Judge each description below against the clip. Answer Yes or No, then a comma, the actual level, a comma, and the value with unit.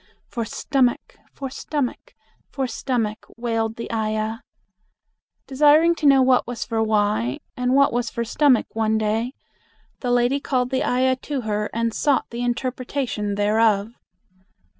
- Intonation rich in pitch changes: No, average, 3.0 semitones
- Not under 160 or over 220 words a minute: No, average, 140 wpm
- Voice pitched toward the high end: Yes, high, 240 Hz